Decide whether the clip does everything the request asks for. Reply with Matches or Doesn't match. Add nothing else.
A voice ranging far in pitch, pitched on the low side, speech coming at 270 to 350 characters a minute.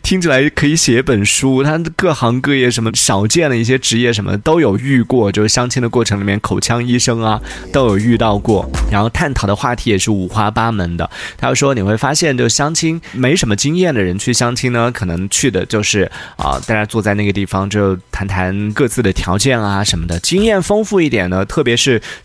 Doesn't match